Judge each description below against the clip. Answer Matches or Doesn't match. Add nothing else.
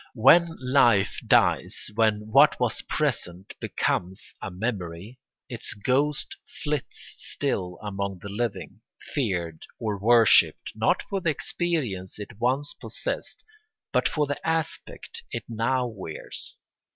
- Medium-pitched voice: Doesn't match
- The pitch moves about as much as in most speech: Doesn't match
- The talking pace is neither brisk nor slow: Doesn't match